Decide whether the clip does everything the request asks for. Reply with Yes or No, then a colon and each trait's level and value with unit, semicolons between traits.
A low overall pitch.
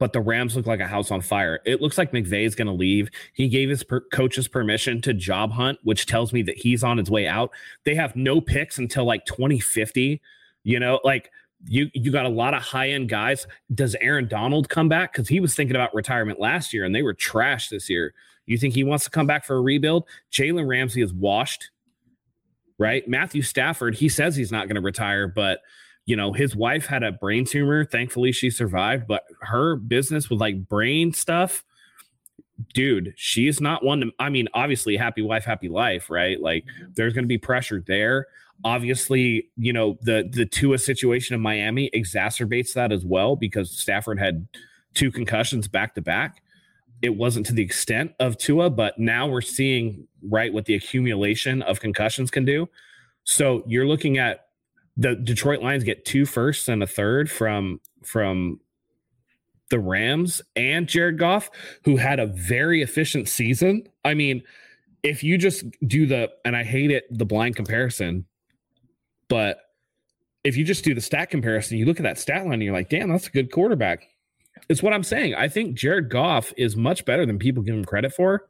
Yes: low, 125 Hz